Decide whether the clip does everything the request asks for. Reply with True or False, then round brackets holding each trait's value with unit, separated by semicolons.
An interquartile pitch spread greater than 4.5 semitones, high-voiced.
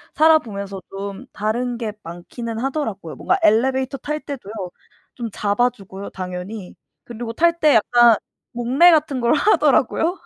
True (5.3 semitones; 235 Hz)